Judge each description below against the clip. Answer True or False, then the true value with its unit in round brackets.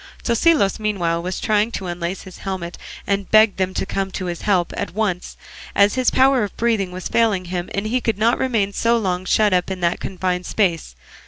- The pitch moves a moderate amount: True (3.2 semitones)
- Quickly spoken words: True (215 wpm)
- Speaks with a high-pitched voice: True (195 Hz)